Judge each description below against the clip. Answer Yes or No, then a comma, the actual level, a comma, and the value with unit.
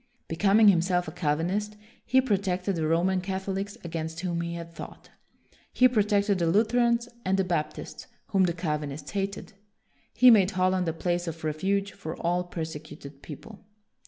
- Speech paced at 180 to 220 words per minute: No, average, 165 wpm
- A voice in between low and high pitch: Yes, medium, 180 Hz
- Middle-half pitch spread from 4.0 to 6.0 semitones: No, average, 3.4 semitones